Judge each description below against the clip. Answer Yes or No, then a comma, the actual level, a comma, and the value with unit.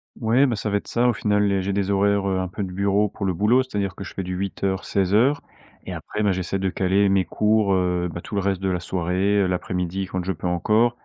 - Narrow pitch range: Yes, narrow, 1.9 semitones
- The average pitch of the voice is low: Yes, low, 100 Hz